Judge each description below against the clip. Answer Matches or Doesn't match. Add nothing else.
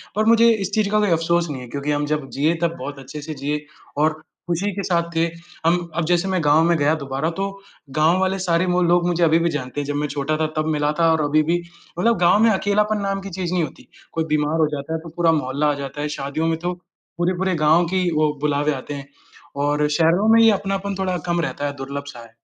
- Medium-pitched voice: Matches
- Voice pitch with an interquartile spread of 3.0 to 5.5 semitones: Matches